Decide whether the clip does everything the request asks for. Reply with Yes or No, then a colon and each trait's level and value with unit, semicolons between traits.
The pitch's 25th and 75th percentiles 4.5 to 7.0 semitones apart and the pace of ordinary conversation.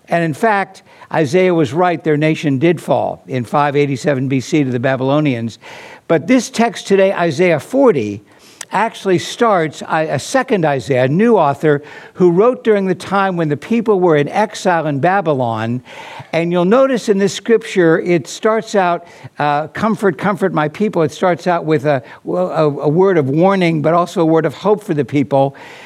Yes: average, 5.1 semitones; average, 175 wpm